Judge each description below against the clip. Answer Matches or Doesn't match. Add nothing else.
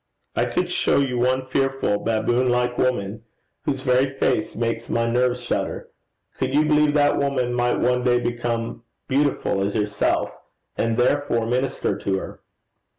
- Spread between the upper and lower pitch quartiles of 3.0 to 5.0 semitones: Doesn't match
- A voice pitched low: Matches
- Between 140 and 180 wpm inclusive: Matches